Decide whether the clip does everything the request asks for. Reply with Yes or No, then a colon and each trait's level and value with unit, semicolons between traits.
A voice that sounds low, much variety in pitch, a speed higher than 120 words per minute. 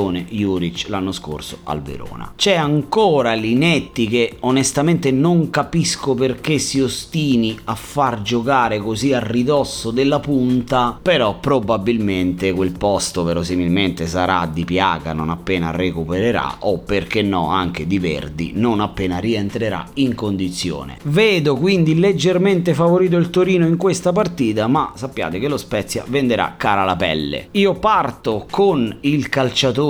Yes: low, 115 Hz; wide, 7.7 semitones; average, 135 wpm